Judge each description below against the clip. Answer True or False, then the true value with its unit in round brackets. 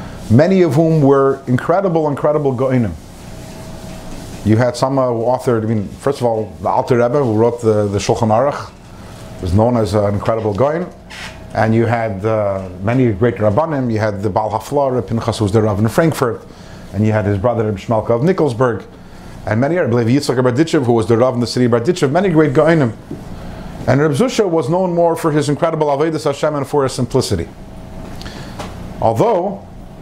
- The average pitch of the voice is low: True (120 Hz)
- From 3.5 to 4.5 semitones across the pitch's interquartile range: False (5.0 semitones)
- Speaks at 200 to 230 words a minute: False (190 wpm)